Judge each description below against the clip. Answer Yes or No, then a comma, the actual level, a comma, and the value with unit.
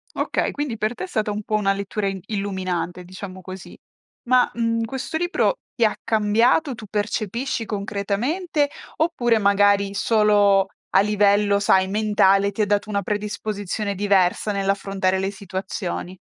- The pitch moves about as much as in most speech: No, narrow, 2.1 semitones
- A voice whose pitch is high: Yes, high, 205 Hz